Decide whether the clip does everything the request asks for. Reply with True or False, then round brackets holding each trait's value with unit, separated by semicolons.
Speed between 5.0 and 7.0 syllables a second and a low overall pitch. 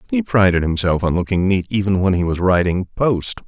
True (5.3 syllables/s; 95 Hz)